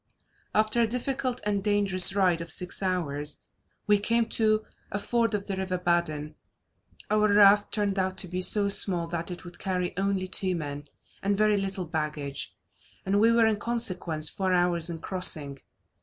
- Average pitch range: Yes, average, 3.2 semitones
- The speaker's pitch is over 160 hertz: Yes, high, 190 Hz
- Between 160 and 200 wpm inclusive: Yes, average, 170 wpm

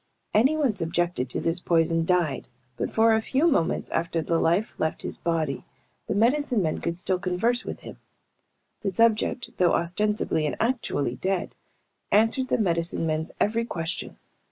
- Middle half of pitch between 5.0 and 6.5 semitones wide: Yes, average, 5.3 semitones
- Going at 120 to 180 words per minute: Yes, average, 155 wpm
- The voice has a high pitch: No, medium, 180 Hz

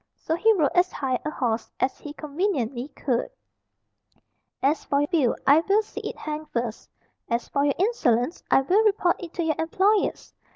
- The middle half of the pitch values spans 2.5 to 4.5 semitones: No, average, 5.2 semitones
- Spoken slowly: No, average, 180 wpm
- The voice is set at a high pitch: Yes, very high, 300 Hz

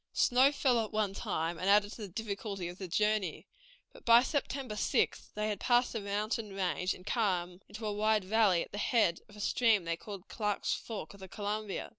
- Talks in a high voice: Yes, high, 210 Hz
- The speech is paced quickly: Yes, fast, 215 wpm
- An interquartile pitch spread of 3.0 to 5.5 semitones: No, narrow, 2.6 semitones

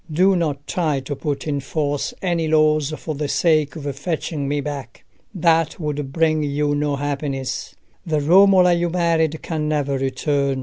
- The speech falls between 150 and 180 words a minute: Yes, average, 165 wpm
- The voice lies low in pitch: No, medium, 150 Hz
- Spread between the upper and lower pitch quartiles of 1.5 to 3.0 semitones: Yes, narrow, 2.4 semitones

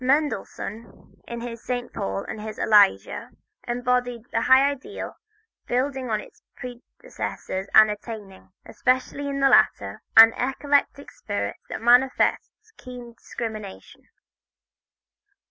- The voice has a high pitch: Yes, high, 245 Hz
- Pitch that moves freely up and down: No, average, 3.3 semitones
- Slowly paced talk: Yes, slow, 110 wpm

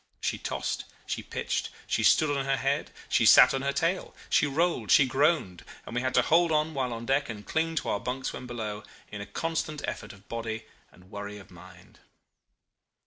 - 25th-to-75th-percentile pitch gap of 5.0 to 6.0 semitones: Yes, wide, 5.6 semitones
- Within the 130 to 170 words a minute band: No, average, 200 wpm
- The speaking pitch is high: No, low, 135 Hz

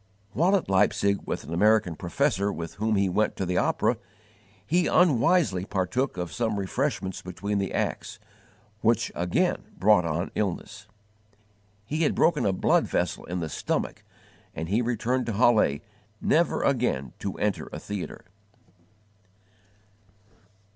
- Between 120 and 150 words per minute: Yes, average, 140 wpm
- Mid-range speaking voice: No, low, 100 Hz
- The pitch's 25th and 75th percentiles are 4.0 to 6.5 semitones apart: Yes, average, 4.4 semitones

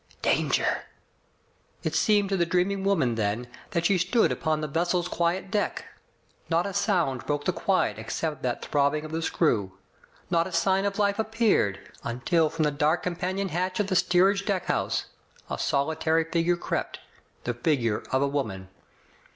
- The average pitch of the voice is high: No, medium, 170 Hz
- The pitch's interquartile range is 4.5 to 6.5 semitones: Yes, average, 4.9 semitones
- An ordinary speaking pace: Yes, average, 165 wpm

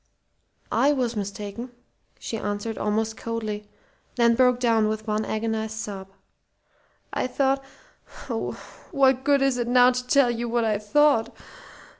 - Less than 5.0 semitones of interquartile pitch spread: Yes, average, 2.7 semitones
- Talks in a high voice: Yes, high, 230 Hz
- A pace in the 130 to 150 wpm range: Yes, average, 140 wpm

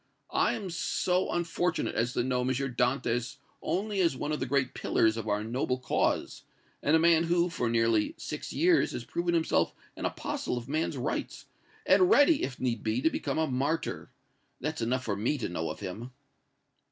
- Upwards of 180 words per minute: Yes, average, 190 wpm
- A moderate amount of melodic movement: No, wide, 5.9 semitones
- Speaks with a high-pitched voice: No, low, 130 Hz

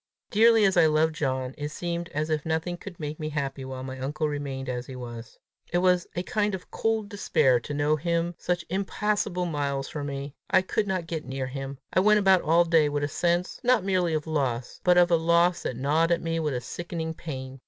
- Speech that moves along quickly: Yes, fast, 225 wpm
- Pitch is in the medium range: Yes, medium, 160 Hz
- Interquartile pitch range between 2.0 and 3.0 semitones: No, average, 4.1 semitones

